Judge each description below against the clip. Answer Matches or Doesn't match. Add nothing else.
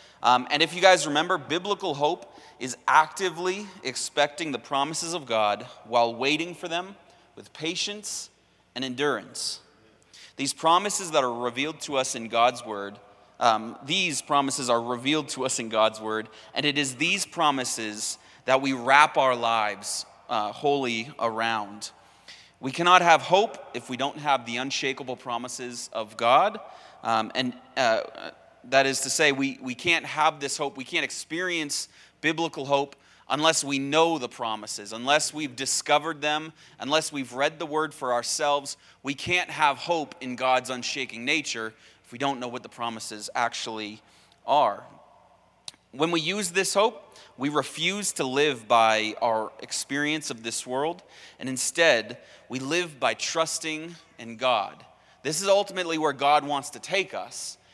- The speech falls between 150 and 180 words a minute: Matches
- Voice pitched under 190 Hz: Matches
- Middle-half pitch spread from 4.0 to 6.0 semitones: Matches